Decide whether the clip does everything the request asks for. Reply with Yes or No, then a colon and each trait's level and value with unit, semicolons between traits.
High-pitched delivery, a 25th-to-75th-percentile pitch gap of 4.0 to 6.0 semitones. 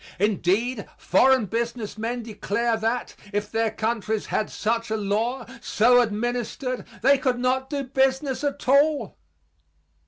No: high, 235 Hz; average, 3.1 semitones